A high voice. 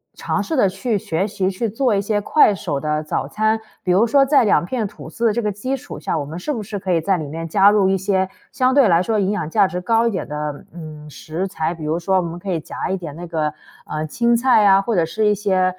Yes: high, 195 Hz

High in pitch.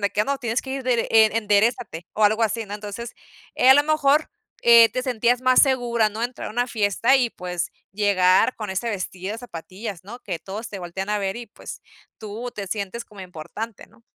Yes: high, 220 Hz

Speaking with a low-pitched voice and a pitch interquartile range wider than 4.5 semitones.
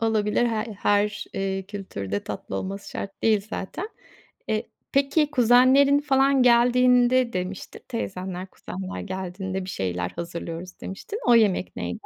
No: high, 205 Hz; average, 5.0 semitones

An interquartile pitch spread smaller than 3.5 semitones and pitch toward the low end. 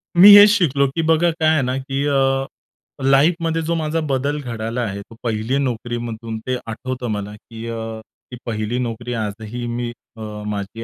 No: average, 3.8 semitones; low, 125 Hz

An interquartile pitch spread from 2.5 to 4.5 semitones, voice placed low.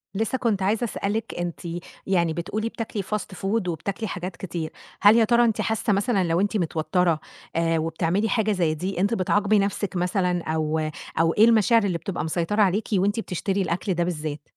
No: average, 3.7 semitones; high, 190 Hz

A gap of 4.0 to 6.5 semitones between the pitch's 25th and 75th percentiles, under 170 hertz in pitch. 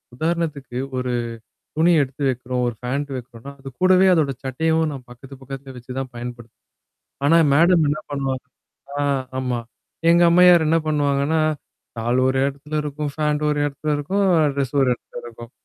No: average, 3.4 semitones; medium, 140 Hz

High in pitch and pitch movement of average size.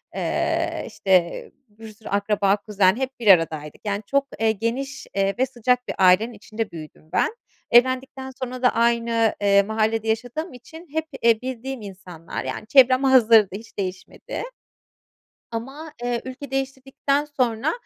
Yes: high, 230 Hz; average, 4.3 semitones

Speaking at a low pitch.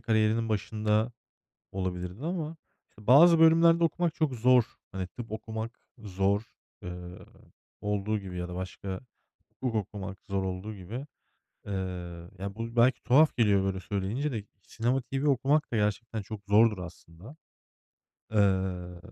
Yes: low, 110 Hz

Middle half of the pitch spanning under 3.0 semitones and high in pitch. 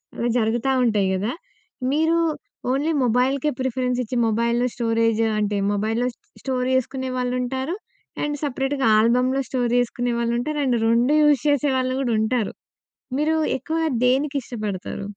Yes: narrow, 2.6 semitones; very high, 250 Hz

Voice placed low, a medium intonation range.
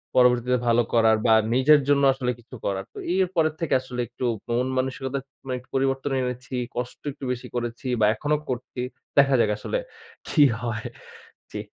No: low, 125 Hz; narrow, 2.1 semitones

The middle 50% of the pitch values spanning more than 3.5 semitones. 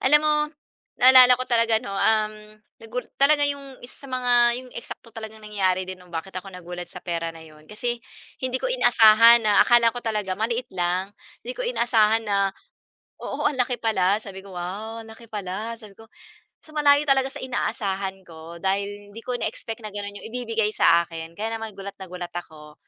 Yes: average, 4.2 semitones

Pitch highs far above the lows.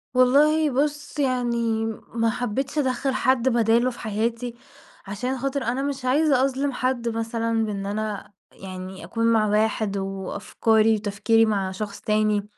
No: average, 3.4 semitones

